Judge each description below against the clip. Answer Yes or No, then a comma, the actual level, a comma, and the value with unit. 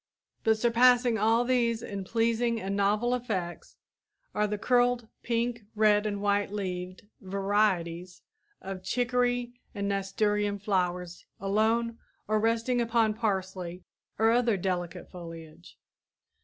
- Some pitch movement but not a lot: Yes, average, 3.4 semitones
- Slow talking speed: Yes, slow, 115 wpm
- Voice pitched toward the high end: Yes, high, 210 Hz